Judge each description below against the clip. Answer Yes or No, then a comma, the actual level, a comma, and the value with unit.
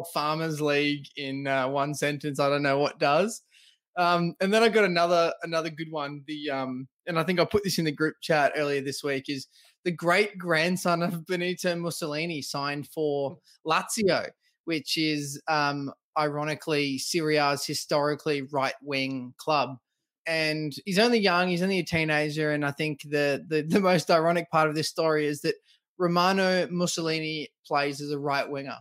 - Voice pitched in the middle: Yes, medium, 155 Hz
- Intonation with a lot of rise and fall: No, average, 3.1 semitones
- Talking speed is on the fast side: No, average, 170 wpm